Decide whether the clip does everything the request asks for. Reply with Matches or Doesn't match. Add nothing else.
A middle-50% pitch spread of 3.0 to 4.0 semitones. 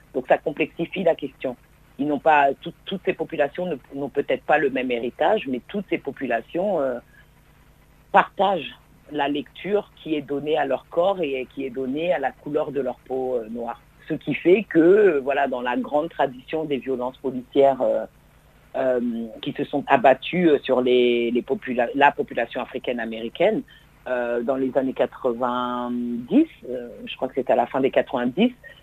Matches